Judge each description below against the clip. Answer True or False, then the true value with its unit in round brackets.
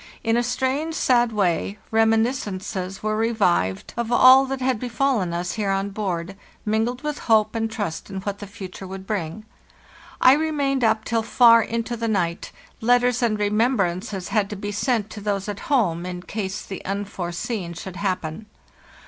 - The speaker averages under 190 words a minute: True (170 wpm)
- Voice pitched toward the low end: False (215 Hz)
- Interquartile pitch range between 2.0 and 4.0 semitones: True (3.6 semitones)